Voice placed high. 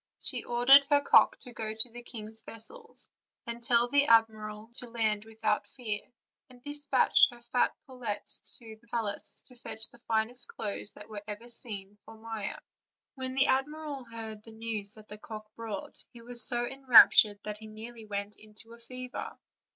Yes: high, 230 Hz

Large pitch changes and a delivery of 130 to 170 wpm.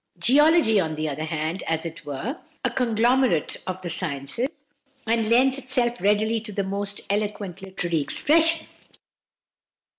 Yes: wide, 6.9 semitones; average, 145 wpm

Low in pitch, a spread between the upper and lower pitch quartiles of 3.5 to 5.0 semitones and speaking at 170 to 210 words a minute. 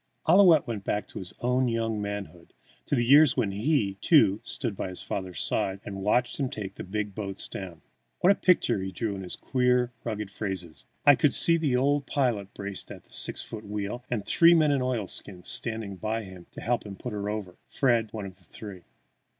Yes: low, 110 Hz; average, 4.3 semitones; fast, 205 wpm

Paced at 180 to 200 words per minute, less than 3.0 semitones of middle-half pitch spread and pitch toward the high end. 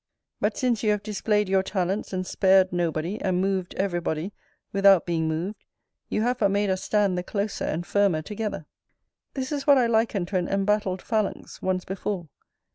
Yes: average, 185 wpm; narrow, 2.5 semitones; high, 195 Hz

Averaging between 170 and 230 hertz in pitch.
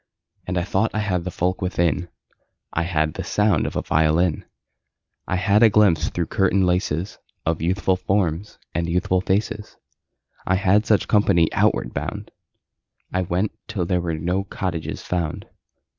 No: very low, 90 Hz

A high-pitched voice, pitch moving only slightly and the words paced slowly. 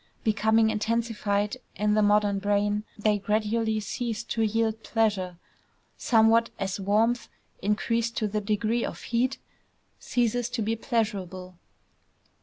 Yes: high, 215 Hz; narrow, 1.7 semitones; slow, 120 wpm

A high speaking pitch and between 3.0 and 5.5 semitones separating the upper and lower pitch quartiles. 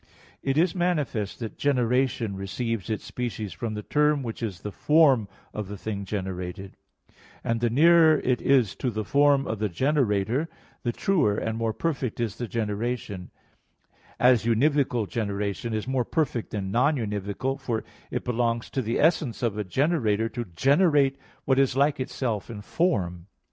No: low, 120 Hz; average, 4.6 semitones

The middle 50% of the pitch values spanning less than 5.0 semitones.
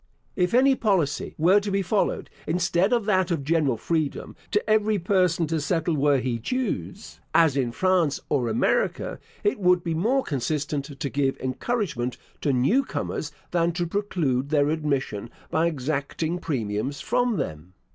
No: average, 5.3 semitones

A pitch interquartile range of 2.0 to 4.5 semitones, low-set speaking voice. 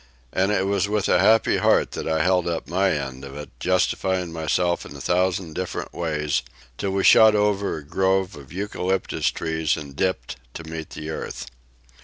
Yes: average, 3.6 semitones; very low, 90 Hz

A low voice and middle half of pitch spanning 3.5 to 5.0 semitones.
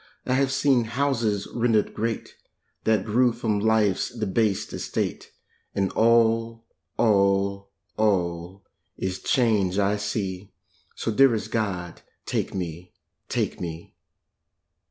No: low, 105 Hz; average, 3.0 semitones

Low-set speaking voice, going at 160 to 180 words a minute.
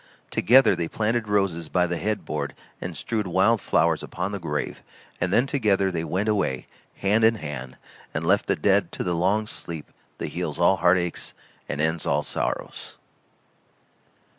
Yes: very low, 95 Hz; average, 165 wpm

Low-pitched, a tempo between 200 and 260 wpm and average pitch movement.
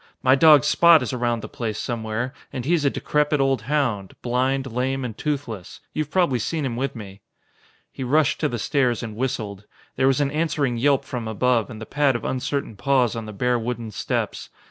Yes: low, 125 Hz; fast, 205 wpm; average, 3.4 semitones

